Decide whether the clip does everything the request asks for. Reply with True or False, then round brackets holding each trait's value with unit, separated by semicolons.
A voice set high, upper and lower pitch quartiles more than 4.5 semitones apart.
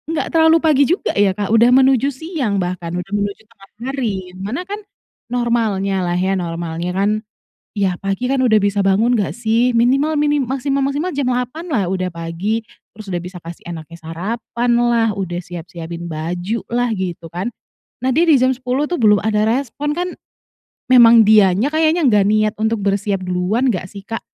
True (215 Hz; 5.6 semitones)